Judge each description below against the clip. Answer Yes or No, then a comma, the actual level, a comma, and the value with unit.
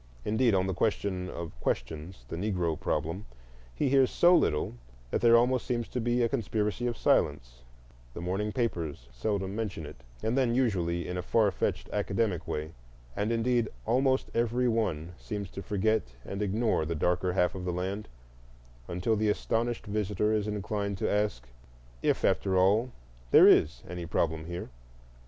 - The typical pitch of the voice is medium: No, low, 100 Hz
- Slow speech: No, average, 160 wpm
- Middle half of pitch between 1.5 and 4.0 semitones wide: No, average, 4.6 semitones